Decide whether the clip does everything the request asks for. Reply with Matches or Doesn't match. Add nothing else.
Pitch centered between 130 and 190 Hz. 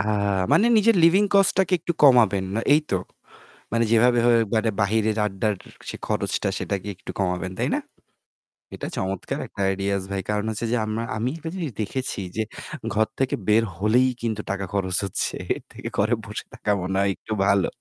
Doesn't match